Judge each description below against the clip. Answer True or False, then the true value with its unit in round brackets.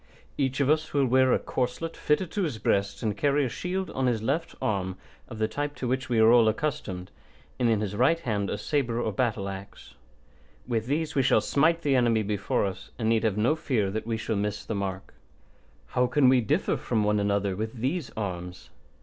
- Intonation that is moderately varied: True (4.8 semitones)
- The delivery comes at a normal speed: False (220 wpm)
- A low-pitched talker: True (115 Hz)